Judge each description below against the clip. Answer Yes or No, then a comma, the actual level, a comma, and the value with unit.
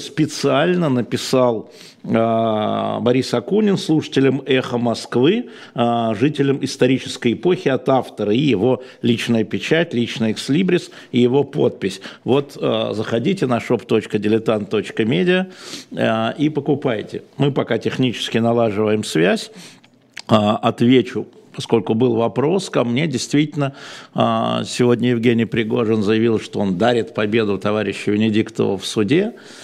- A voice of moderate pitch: No, low, 120 Hz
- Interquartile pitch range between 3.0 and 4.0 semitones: Yes, average, 3.7 semitones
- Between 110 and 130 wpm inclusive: Yes, average, 115 wpm